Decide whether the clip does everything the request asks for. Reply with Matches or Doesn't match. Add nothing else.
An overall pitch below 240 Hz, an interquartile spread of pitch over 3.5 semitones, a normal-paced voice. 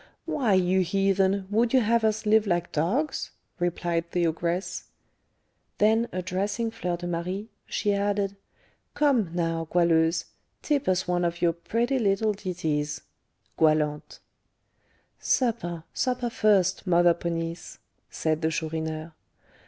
Doesn't match